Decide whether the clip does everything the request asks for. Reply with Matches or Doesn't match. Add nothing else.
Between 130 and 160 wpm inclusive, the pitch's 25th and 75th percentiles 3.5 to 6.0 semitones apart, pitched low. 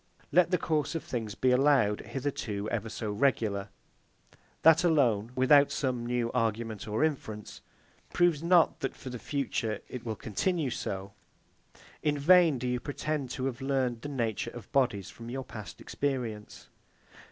Matches